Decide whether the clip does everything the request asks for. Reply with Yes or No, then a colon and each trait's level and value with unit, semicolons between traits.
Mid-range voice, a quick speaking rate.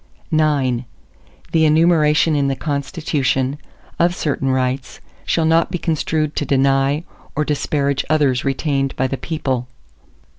No: medium, 145 Hz; slow, 135 wpm